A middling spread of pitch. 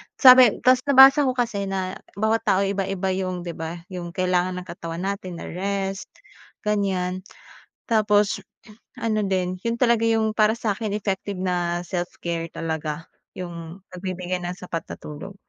Yes: average, 3.0 semitones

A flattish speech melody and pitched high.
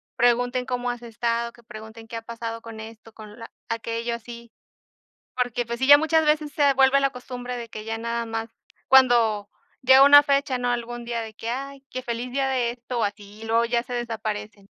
Yes: narrow, 1.9 semitones; high, 235 Hz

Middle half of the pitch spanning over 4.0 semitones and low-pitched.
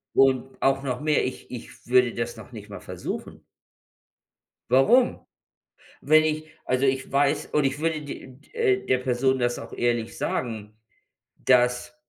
No: narrow, 2.6 semitones; low, 130 Hz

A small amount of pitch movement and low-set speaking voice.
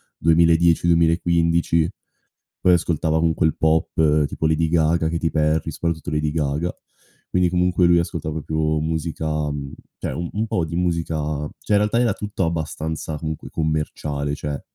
Yes: narrow, 1.6 semitones; very low, 80 Hz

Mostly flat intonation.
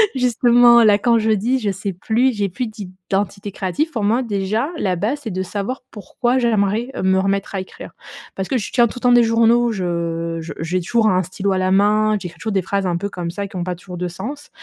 No: average, 3.9 semitones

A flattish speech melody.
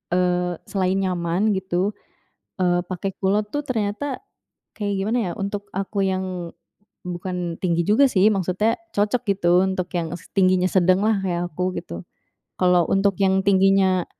Yes: narrow, 2.0 semitones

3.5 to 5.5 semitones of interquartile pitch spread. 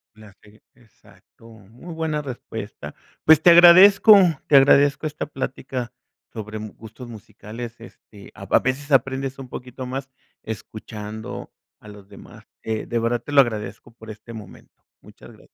Yes: average, 4.2 semitones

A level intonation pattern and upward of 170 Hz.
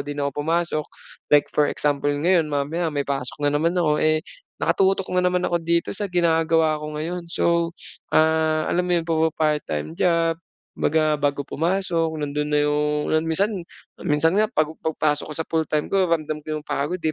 No: narrow, 2.3 semitones; medium, 160 Hz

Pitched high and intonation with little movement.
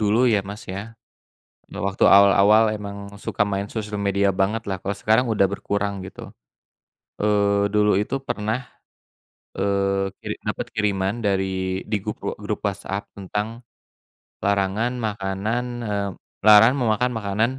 No: low, 100 Hz; narrow, 1.4 semitones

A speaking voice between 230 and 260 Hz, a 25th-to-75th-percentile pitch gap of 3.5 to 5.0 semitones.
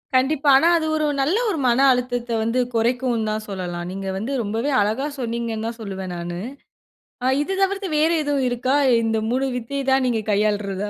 Yes: high, 235 Hz; average, 4.2 semitones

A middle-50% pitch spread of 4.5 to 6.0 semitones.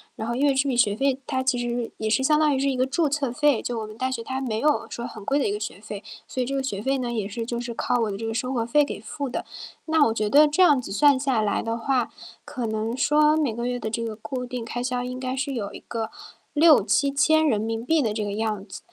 No: average, 3.7 semitones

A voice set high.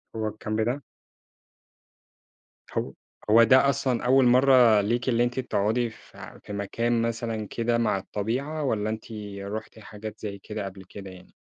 No: low, 110 Hz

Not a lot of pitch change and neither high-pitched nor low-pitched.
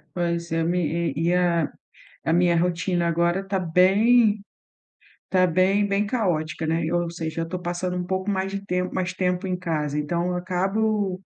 Yes: narrow, 2.1 semitones; medium, 180 Hz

